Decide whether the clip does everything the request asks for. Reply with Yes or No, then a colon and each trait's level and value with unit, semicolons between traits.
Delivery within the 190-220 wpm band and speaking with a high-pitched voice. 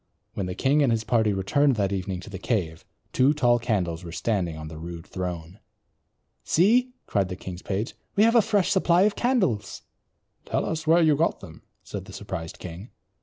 No: average, 195 wpm; low, 105 Hz